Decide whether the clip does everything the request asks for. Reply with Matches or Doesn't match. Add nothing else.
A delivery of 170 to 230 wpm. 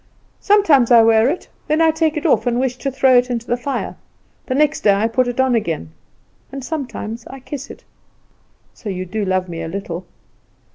Matches